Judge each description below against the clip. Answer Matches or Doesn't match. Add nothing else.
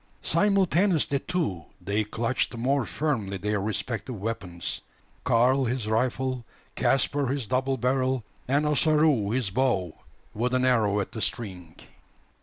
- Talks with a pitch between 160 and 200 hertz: Doesn't match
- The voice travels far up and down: Doesn't match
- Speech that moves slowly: Matches